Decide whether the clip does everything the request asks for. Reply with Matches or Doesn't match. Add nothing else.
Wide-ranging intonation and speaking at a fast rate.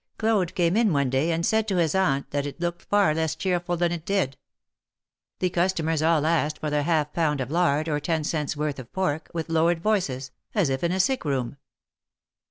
Doesn't match